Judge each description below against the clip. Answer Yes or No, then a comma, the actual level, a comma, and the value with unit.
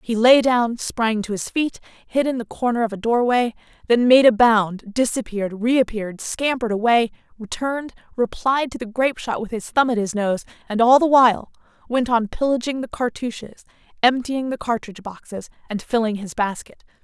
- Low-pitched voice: No, high, 235 Hz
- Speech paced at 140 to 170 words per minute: No, average, 185 wpm